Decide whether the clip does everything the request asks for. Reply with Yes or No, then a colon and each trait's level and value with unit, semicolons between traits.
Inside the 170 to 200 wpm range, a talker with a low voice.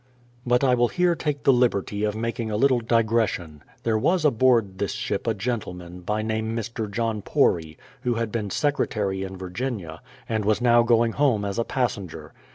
Yes: average, 185 wpm; low, 115 Hz